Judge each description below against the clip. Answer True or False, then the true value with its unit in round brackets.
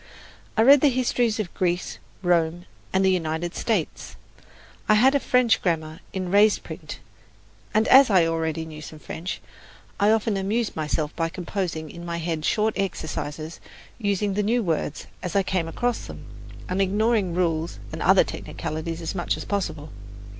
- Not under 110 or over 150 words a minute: False (165 wpm)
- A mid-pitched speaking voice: True (180 Hz)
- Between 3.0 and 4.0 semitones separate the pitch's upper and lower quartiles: False (4.5 semitones)